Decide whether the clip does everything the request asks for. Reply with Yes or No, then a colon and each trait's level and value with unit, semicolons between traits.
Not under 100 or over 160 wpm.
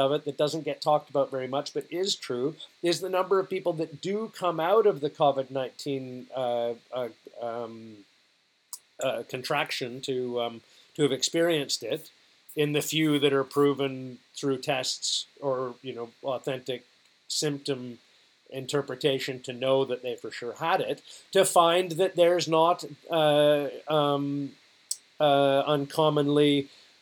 Yes: average, 150 wpm